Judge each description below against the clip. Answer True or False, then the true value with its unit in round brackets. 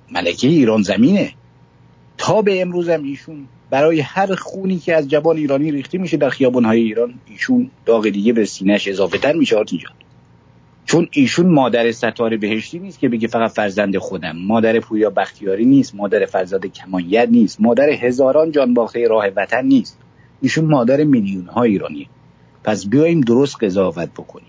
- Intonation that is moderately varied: False (6.8 semitones)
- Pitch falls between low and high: False (125 Hz)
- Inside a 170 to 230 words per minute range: False (155 wpm)